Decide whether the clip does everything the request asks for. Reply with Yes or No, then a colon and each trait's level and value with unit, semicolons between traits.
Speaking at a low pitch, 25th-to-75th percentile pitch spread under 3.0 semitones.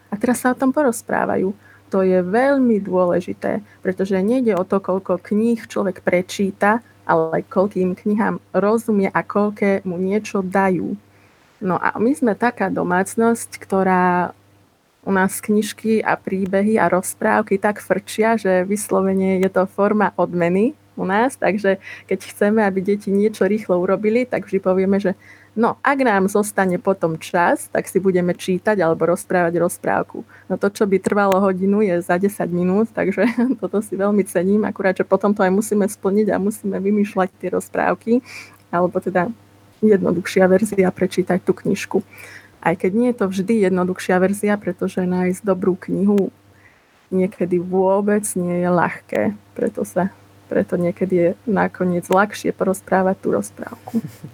No: high, 190 Hz; narrow, 2.4 semitones